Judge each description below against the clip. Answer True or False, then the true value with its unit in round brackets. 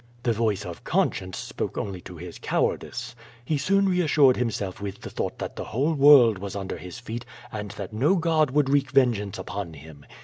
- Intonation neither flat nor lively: False (6.7 semitones)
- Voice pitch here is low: True (115 Hz)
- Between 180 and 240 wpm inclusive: True (195 wpm)